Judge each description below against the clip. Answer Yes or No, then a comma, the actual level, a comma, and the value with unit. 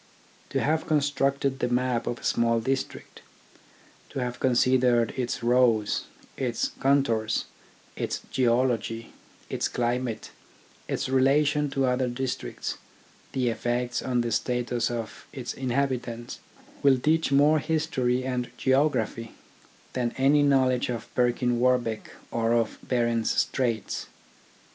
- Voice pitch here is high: No, low, 125 Hz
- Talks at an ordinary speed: No, slow, 125 wpm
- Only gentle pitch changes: Yes, narrow, 2.1 semitones